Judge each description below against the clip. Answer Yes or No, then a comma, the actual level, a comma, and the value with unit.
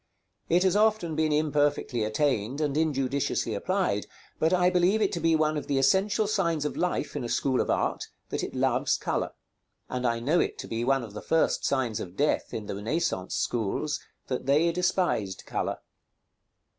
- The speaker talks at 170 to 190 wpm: Yes, average, 185 wpm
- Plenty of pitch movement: Yes, wide, 6.0 semitones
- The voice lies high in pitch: No, medium, 150 Hz